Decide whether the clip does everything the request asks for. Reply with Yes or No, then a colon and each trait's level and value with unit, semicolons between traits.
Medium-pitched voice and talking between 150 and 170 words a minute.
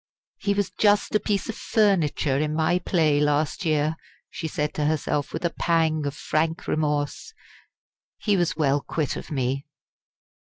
Yes: medium, 155 Hz; average, 160 wpm